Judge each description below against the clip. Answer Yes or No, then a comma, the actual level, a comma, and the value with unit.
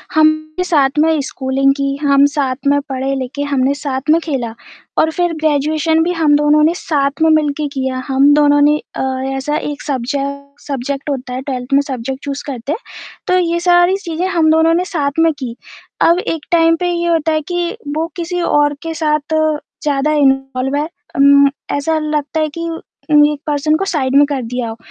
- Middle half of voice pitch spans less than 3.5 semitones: Yes, average, 2.7 semitones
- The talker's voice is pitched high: Yes, very high, 295 Hz